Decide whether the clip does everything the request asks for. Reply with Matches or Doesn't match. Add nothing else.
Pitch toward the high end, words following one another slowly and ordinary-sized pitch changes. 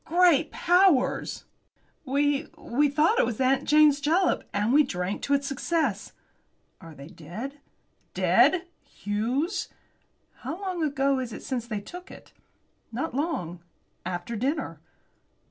Doesn't match